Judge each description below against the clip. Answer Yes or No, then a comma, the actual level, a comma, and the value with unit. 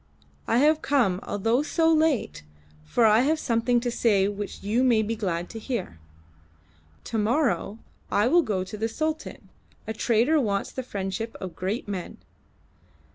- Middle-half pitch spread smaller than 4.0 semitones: No, average, 4.3 semitones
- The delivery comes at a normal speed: Yes, average, 160 wpm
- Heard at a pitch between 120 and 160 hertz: No, high, 225 Hz